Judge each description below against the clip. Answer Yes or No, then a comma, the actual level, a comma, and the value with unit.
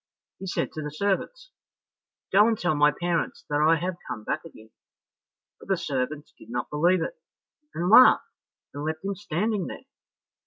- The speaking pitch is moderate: Yes, medium, 170 Hz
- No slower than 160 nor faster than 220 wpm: Yes, average, 170 wpm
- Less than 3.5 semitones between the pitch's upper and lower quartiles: No, average, 4.9 semitones